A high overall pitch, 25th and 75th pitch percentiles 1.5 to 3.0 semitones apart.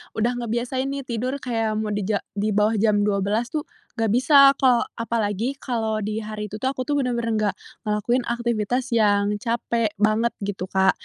Yes: high, 225 Hz; average, 2.7 semitones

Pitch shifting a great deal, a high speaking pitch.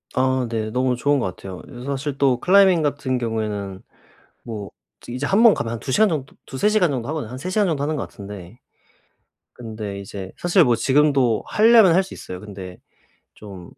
No: wide, 6.2 semitones; low, 130 Hz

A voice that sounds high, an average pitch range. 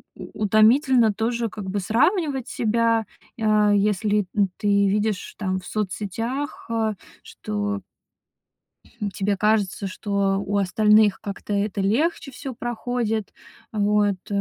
No: high, 210 Hz; narrow, 2.2 semitones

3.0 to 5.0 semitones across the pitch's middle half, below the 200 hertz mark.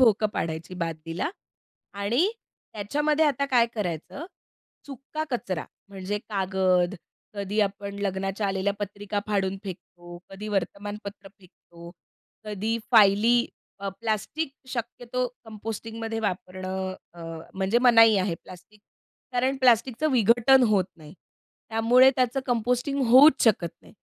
No: average, 4.0 semitones; high, 210 Hz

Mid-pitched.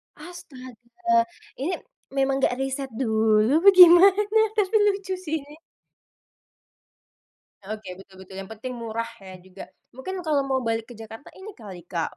No: very high, 260 Hz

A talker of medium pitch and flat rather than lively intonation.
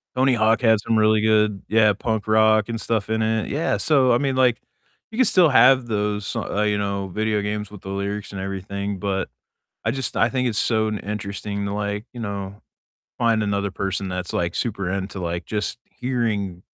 No: low, 105 Hz; narrow, 2.2 semitones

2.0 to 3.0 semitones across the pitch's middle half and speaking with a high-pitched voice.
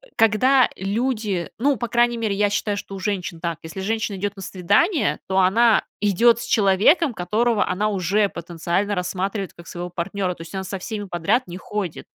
No: average, 3.5 semitones; high, 200 Hz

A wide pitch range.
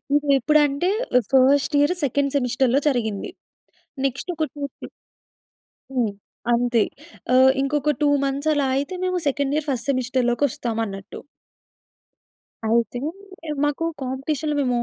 No: average, 3.0 semitones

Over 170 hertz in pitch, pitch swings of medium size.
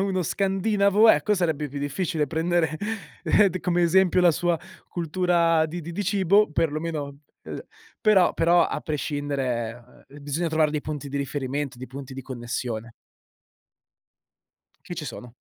No: medium, 160 Hz; average, 4.0 semitones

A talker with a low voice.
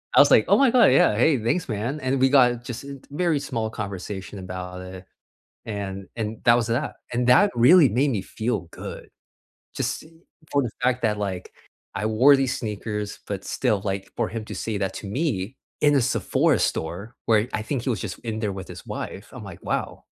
Yes: low, 110 Hz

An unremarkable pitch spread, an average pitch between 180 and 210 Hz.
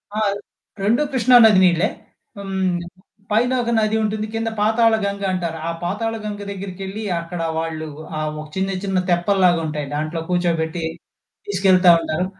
Yes: average, 3.7 semitones; high, 190 Hz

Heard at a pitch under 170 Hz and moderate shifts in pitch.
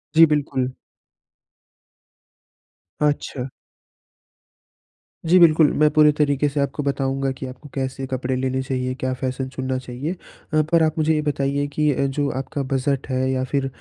No: low, 135 Hz; narrow, 2.3 semitones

